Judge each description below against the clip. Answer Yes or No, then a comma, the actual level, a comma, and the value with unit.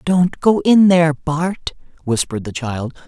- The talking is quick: No, average, 155 wpm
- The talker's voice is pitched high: No, medium, 160 Hz